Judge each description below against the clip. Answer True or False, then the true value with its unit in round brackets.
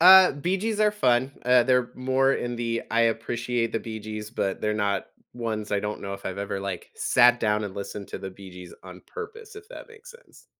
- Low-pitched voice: True (115 Hz)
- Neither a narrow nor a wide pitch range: True (5.0 semitones)